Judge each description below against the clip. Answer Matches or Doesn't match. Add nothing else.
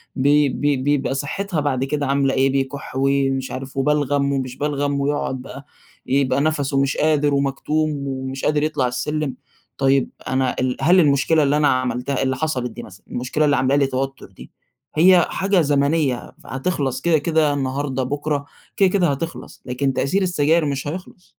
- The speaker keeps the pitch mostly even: Matches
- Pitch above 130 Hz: Matches